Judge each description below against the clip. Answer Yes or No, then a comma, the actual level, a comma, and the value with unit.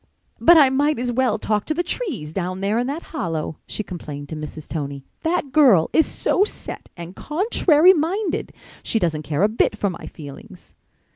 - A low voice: No, high, 220 Hz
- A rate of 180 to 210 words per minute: Yes, average, 190 wpm